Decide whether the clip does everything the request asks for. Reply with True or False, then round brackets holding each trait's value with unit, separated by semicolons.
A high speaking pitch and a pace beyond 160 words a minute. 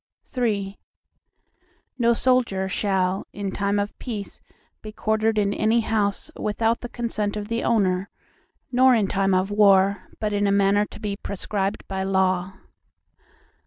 False (205 Hz; 145 wpm)